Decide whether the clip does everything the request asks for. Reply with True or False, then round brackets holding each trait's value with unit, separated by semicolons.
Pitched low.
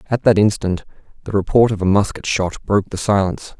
True (100 Hz)